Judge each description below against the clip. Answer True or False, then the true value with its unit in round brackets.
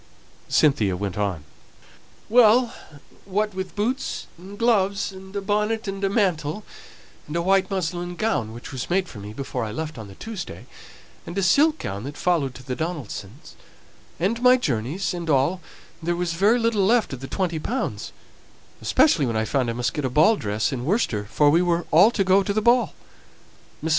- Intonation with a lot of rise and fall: True (7.4 semitones)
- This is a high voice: False (175 Hz)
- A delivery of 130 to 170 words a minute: False (190 wpm)